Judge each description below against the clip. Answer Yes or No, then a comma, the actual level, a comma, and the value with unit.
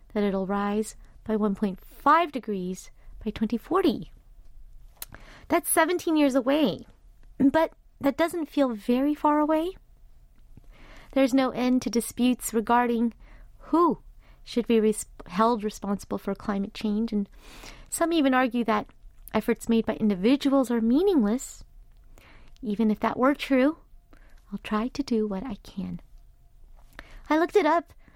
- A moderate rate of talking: No, slow, 130 wpm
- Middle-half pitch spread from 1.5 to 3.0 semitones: No, average, 5.0 semitones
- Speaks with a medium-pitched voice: No, high, 240 Hz